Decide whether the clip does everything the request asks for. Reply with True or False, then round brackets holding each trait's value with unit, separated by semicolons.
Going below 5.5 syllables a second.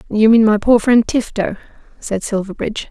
True (5.3 syllables/s)